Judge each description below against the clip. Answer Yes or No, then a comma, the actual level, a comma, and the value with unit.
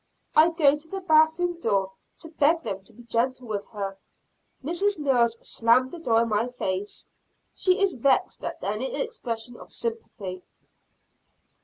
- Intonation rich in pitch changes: Yes, wide, 6.9 semitones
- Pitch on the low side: No, very high, 260 Hz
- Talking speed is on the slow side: No, average, 160 wpm